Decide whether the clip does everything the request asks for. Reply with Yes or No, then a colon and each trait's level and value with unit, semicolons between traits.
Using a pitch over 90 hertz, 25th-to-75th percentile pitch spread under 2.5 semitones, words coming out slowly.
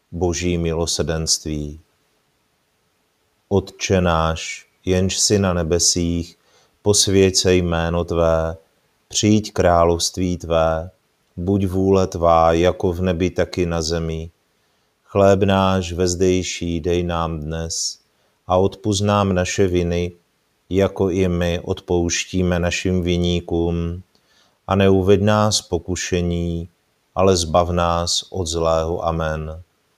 No: very low, 85 Hz; narrow, 2.0 semitones; slow, 105 wpm